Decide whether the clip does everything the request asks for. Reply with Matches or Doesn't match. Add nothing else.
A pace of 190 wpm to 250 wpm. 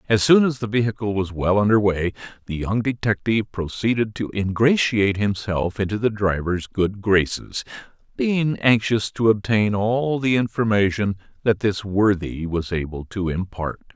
Doesn't match